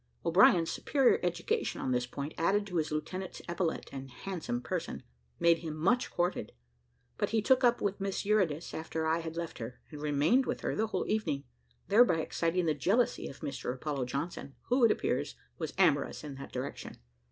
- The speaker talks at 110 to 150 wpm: No, average, 185 wpm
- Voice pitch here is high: No, medium, 165 Hz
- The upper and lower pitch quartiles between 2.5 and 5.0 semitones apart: No, wide, 5.4 semitones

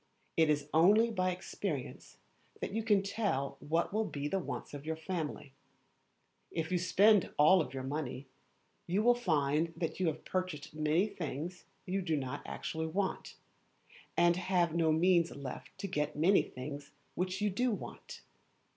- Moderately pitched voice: Yes, medium, 170 Hz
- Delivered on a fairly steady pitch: No, average, 4.1 semitones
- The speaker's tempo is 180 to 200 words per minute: No, average, 155 wpm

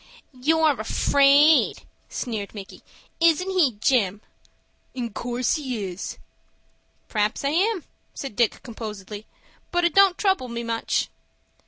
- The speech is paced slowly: Yes, slow, 120 wpm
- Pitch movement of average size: No, wide, 6.8 semitones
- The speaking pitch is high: Yes, very high, 250 Hz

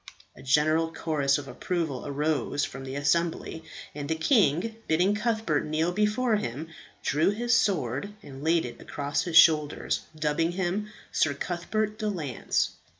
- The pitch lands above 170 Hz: No, medium, 160 Hz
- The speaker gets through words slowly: No, average, 150 wpm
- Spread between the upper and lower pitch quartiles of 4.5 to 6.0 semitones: Yes, average, 5.2 semitones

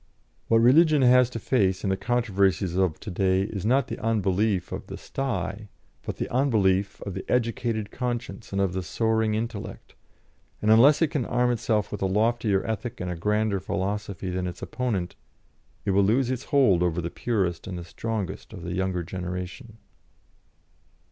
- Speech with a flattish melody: No, average, 4.0 semitones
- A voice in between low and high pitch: No, low, 105 Hz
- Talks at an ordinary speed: Yes, average, 175 wpm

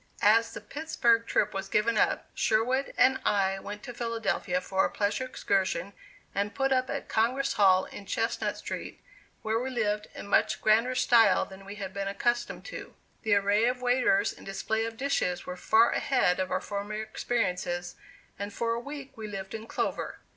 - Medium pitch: No, high, 220 Hz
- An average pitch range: Yes, average, 3.3 semitones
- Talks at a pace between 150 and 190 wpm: Yes, average, 185 wpm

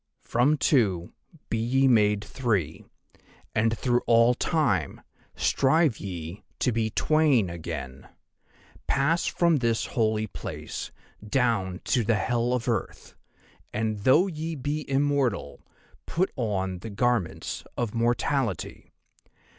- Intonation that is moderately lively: Yes, average, 4.6 semitones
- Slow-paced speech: Yes, slow, 115 wpm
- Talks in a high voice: No, low, 115 Hz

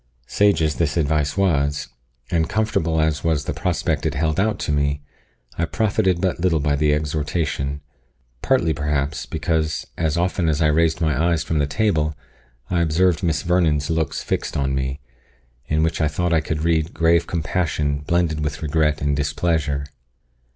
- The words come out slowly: No, average, 170 wpm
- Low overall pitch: Yes, very low, 80 Hz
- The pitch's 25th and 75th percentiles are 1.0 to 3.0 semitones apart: Yes, narrow, 2.4 semitones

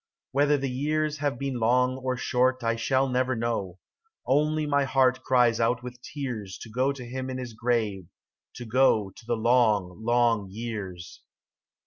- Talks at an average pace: Yes, average, 165 wpm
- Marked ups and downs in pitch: No, narrow, 2.5 semitones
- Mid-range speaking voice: No, low, 125 Hz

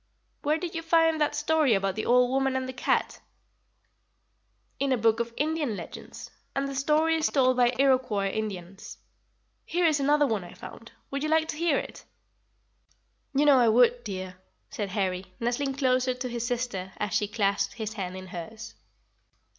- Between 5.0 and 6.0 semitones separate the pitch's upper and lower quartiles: Yes, wide, 5.4 semitones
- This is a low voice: No, very high, 250 Hz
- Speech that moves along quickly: No, average, 180 wpm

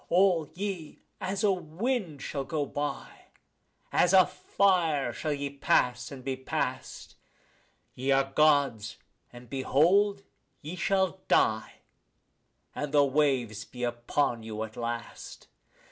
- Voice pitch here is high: No, medium, 145 Hz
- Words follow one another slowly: Yes, slow, 125 wpm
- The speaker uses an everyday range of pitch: No, wide, 6.2 semitones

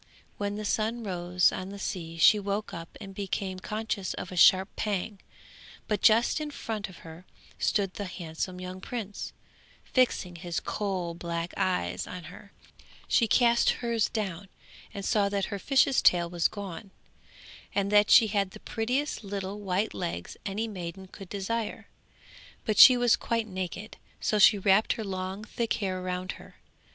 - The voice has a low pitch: No, high, 200 Hz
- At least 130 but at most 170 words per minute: Yes, average, 165 wpm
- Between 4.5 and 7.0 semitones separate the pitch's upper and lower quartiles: No, average, 2.8 semitones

